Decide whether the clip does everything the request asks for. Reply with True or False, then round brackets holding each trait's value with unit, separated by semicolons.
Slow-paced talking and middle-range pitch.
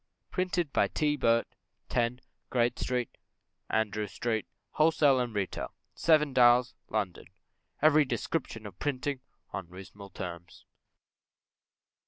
False (110 wpm; 120 Hz)